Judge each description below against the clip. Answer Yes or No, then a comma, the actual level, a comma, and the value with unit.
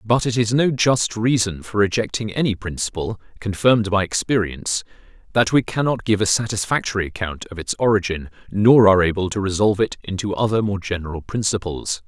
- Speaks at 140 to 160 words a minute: No, average, 170 wpm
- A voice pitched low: Yes, low, 105 Hz